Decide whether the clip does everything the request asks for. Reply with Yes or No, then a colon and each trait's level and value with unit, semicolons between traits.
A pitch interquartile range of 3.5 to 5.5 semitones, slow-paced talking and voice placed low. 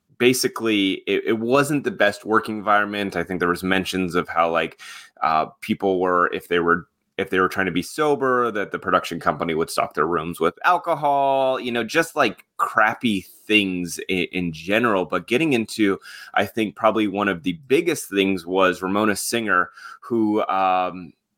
No: average, 4.1 semitones; average, 180 wpm; low, 100 Hz